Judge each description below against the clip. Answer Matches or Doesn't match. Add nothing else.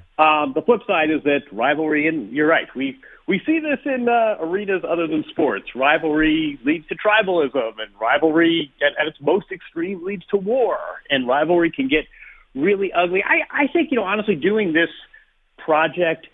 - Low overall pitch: Doesn't match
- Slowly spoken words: Doesn't match